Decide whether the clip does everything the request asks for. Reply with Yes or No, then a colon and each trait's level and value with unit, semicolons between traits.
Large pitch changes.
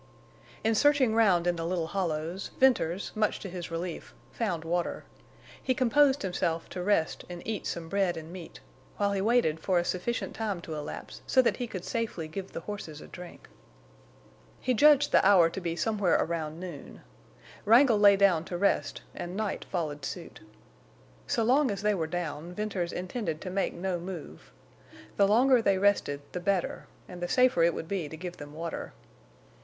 No: average, 4.0 semitones